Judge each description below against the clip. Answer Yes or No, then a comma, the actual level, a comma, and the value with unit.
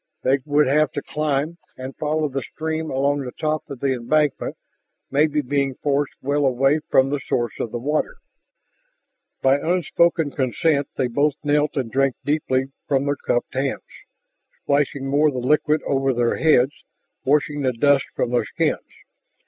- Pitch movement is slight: Yes, narrow, 2.2 semitones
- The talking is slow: No, average, 165 wpm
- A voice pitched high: No, medium, 140 Hz